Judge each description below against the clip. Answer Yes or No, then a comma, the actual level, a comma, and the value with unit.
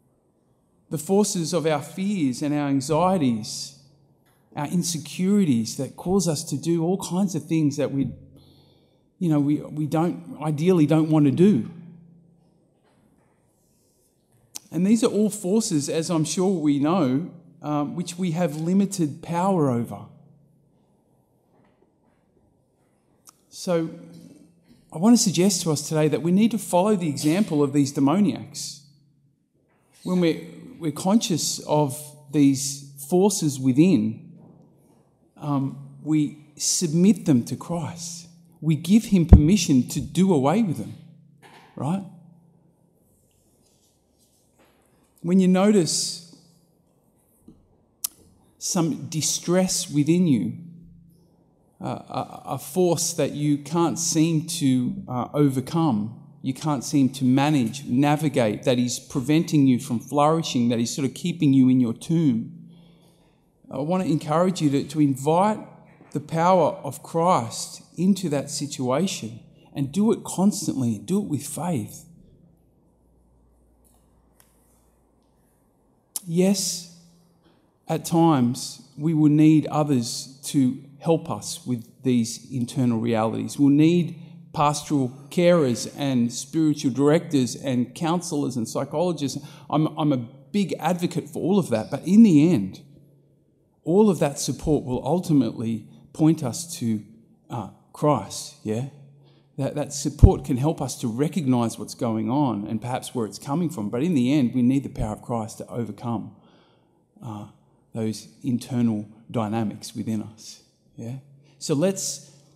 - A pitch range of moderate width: Yes, average, 4.1 semitones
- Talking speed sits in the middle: No, slow, 125 wpm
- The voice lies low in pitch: No, medium, 150 Hz